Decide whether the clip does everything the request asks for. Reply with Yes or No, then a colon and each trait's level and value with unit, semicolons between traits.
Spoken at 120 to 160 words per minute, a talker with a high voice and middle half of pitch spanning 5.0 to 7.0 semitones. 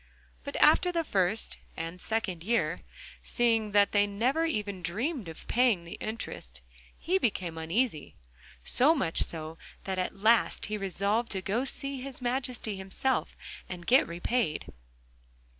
Yes: average, 145 wpm; high, 210 Hz; wide, 5.6 semitones